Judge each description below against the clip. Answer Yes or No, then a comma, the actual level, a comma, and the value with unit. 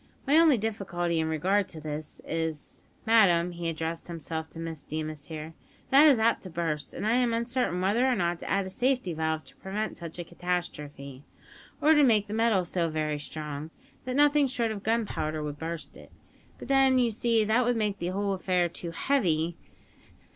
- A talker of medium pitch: Yes, medium, 180 Hz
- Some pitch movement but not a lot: No, wide, 6.1 semitones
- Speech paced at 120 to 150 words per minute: No, average, 200 wpm